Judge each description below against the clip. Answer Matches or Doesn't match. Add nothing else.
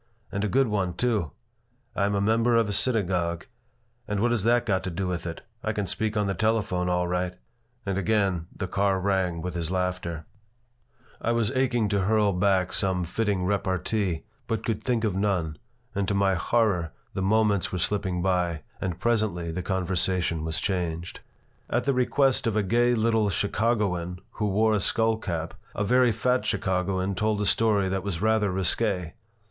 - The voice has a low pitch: Matches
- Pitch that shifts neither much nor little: Matches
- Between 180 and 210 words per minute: Matches